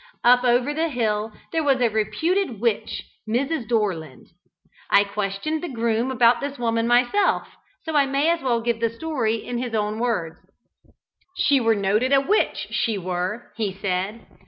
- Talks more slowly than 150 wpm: No, average, 165 wpm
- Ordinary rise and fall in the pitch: Yes, average, 4.2 semitones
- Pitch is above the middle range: Yes, high, 235 Hz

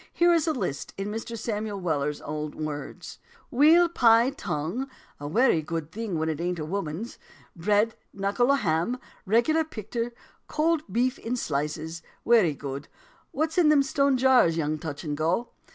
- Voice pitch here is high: Yes, high, 205 Hz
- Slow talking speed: No, average, 165 wpm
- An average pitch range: No, wide, 8.4 semitones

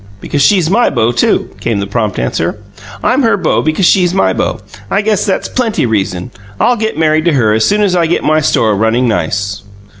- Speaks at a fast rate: Yes, fast, 210 wpm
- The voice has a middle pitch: Yes, medium, 155 Hz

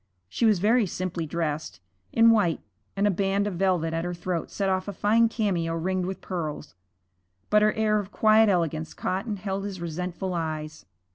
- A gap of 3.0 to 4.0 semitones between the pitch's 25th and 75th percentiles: Yes, average, 3.7 semitones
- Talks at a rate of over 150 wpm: Yes, average, 190 wpm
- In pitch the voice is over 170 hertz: Yes, medium, 185 Hz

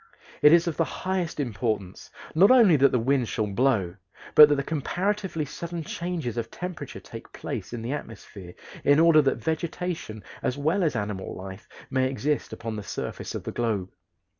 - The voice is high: No, medium, 140 Hz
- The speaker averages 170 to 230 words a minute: Yes, average, 175 wpm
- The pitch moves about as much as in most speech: No, wide, 6.8 semitones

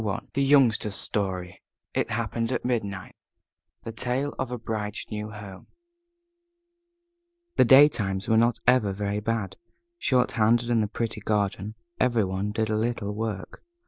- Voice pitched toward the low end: Yes, low, 110 Hz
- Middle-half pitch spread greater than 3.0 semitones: No, narrow, 2.6 semitones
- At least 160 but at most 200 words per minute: No, average, 145 wpm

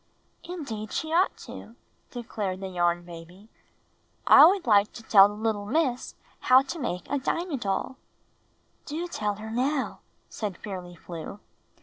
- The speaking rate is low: No, average, 145 wpm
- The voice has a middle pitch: No, high, 220 Hz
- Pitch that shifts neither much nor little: No, wide, 6.1 semitones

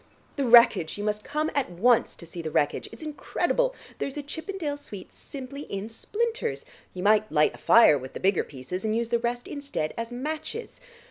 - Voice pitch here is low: No, high, 235 Hz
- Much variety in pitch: Yes, wide, 7.1 semitones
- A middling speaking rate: Yes, average, 195 wpm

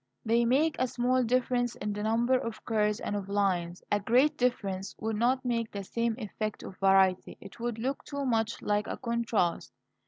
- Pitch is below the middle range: No, high, 225 Hz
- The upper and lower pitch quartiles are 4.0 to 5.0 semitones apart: No, average, 3.1 semitones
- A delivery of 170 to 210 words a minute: Yes, average, 190 wpm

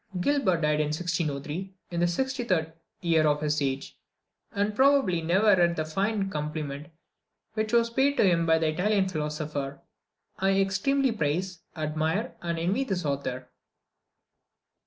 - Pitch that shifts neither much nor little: Yes, average, 4.8 semitones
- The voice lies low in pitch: No, medium, 170 Hz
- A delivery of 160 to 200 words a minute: No, average, 140 wpm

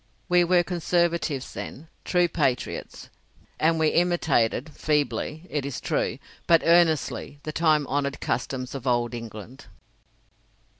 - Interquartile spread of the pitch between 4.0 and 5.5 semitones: Yes, average, 4.3 semitones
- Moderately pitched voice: Yes, medium, 155 Hz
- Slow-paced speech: Yes, slow, 120 wpm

